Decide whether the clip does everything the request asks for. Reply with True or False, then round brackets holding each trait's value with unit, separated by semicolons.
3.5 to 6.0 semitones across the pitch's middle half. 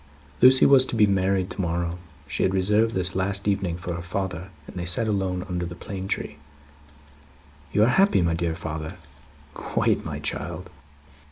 False (2.5 semitones)